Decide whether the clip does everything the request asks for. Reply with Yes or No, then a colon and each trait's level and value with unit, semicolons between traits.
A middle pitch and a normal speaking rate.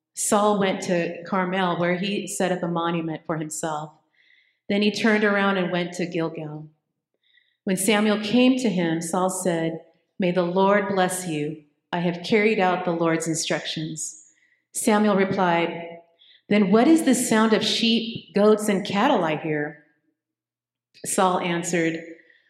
Yes: medium, 180 Hz; average, 145 wpm